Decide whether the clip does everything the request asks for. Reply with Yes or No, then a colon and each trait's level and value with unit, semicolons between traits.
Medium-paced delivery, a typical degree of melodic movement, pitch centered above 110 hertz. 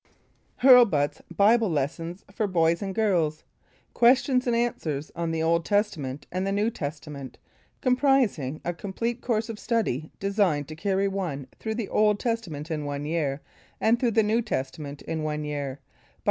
No: average, 165 wpm; wide, 6.6 semitones; medium, 185 Hz